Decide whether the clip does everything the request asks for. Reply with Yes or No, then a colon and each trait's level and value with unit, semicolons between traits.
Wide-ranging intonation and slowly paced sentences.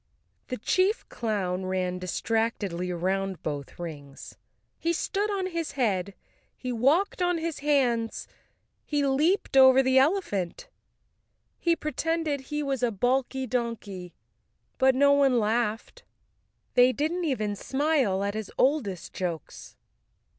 Yes: wide, 7.3 semitones; slow, 125 wpm